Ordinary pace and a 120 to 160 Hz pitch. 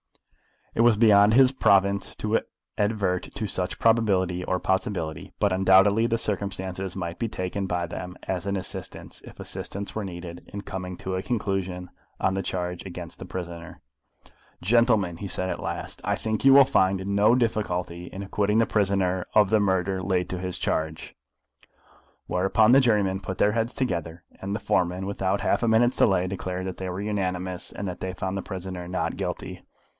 No: average, 180 wpm; very low, 95 Hz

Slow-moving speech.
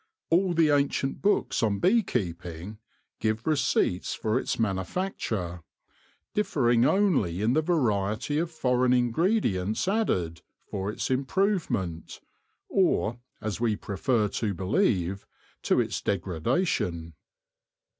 Yes: slow, 110 wpm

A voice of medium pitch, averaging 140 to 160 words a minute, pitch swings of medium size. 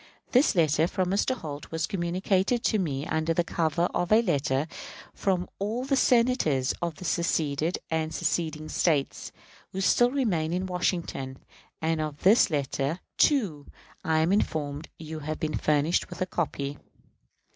Yes: medium, 165 Hz; average, 155 wpm; average, 3.7 semitones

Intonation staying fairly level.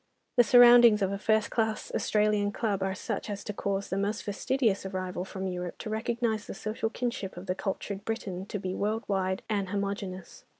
Yes: narrow, 2.3 semitones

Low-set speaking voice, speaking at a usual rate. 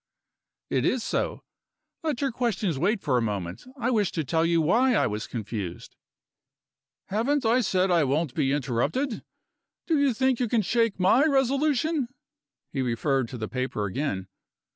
No: medium, 185 Hz; average, 165 wpm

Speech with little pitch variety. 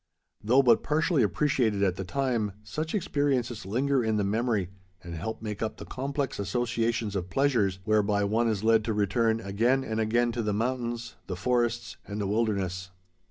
No: average, 3.2 semitones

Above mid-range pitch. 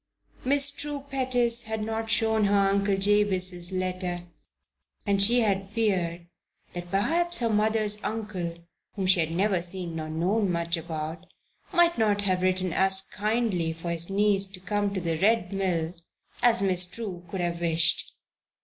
Yes: high, 195 Hz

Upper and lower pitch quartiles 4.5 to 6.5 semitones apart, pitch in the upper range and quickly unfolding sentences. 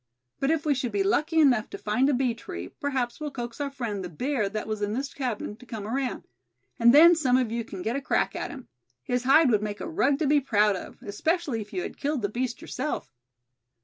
Yes: average, 4.8 semitones; very high, 250 Hz; fast, 245 wpm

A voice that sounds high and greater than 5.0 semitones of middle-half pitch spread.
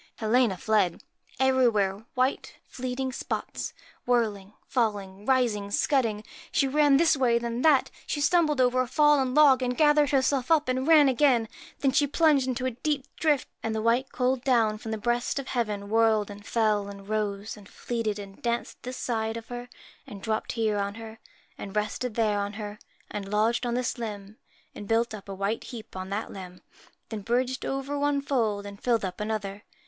No: high, 230 Hz; average, 3.8 semitones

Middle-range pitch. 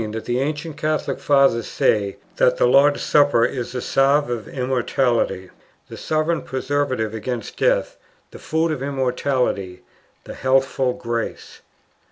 No: low, 130 Hz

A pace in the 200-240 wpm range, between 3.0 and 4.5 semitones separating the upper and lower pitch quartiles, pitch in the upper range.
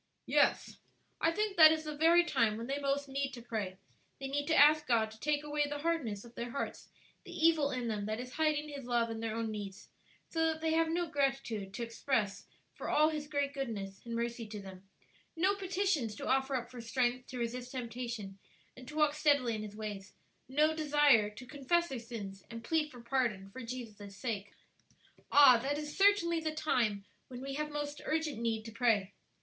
No: fast, 205 wpm; average, 4.9 semitones; very high, 255 Hz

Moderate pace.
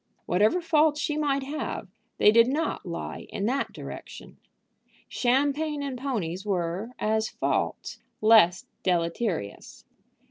No: slow, 115 wpm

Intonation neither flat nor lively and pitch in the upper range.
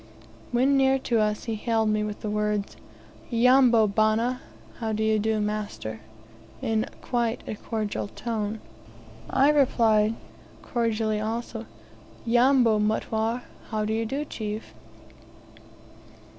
No: narrow, 2.1 semitones; high, 220 Hz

